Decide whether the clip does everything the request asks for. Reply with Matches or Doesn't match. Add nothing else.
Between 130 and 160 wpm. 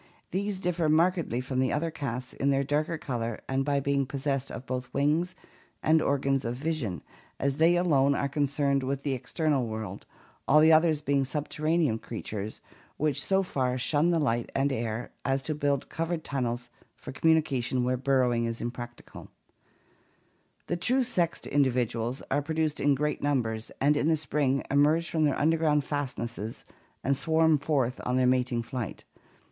Doesn't match